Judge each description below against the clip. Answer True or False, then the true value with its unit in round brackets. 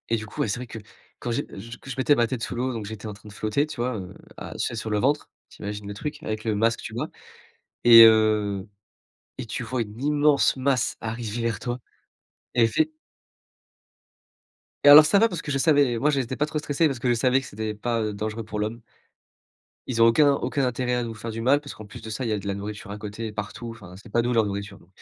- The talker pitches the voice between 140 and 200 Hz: False (115 Hz)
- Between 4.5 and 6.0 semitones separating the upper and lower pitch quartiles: False (3.4 semitones)